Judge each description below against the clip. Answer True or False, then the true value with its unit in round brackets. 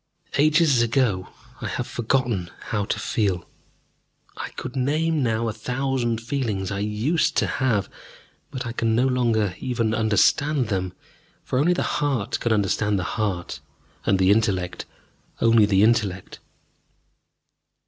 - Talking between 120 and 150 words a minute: True (140 wpm)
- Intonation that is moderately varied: True (4.2 semitones)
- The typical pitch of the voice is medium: False (115 Hz)